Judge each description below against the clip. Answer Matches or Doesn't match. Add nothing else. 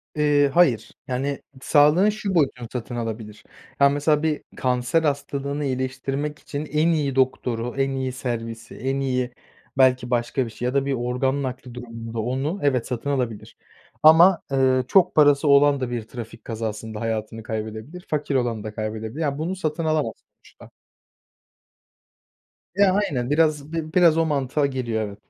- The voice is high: Doesn't match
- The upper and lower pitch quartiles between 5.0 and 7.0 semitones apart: Doesn't match